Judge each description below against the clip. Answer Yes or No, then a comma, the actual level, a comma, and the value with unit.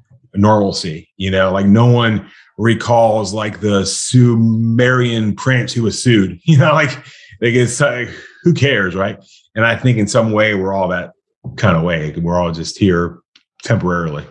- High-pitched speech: No, low, 110 Hz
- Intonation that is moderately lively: Yes, average, 3.8 semitones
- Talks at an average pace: Yes, average, 170 wpm